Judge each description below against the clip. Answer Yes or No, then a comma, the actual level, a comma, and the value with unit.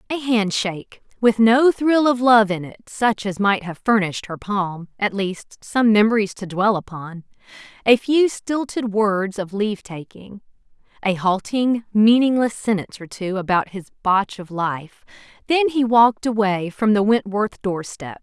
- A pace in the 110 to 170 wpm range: Yes, average, 160 wpm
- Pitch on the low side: No, high, 210 Hz